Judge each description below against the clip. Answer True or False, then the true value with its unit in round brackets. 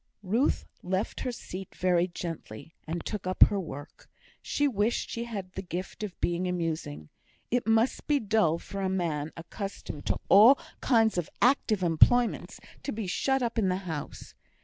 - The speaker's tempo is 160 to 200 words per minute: True (170 wpm)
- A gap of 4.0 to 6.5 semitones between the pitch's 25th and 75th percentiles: True (4.6 semitones)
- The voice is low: False (190 Hz)